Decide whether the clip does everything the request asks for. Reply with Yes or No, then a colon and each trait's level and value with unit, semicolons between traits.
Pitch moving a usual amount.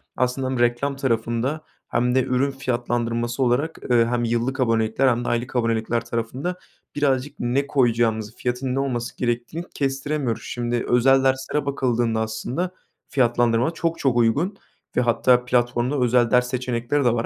No: narrow, 2.2 semitones